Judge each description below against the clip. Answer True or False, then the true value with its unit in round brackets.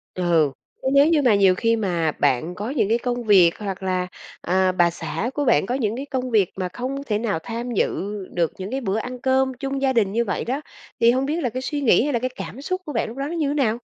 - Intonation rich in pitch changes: True (5.7 semitones)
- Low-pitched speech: False (235 Hz)